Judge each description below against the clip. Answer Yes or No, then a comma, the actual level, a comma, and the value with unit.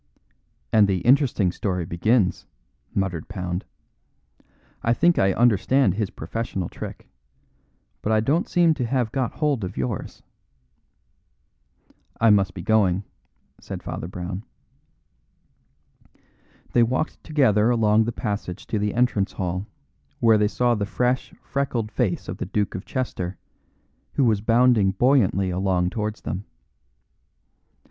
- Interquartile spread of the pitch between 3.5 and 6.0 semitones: Yes, average, 4.4 semitones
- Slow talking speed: Yes, slow, 130 wpm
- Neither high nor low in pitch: No, low, 105 Hz